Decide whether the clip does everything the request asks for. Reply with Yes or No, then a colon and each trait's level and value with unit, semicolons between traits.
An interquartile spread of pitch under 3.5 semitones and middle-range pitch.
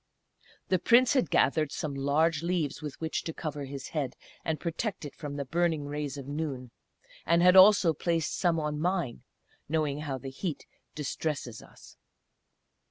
Yes: average, 3.0 semitones; medium, 155 Hz